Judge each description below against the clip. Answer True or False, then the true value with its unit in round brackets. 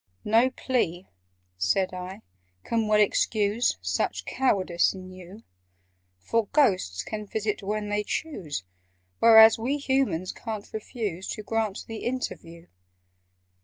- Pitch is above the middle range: True (210 Hz)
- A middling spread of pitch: True (3.6 semitones)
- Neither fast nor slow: False (120 wpm)